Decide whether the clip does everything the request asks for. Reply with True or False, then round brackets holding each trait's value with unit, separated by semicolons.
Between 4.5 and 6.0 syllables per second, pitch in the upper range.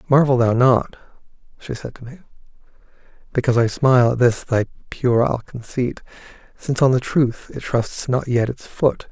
False (5.0 syllables/s; 125 Hz)